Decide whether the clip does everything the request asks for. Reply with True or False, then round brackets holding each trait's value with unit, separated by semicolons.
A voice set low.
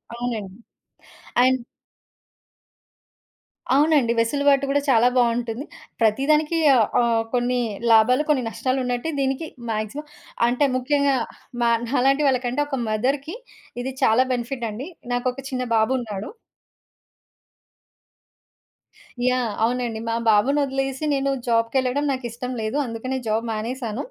False (250 Hz)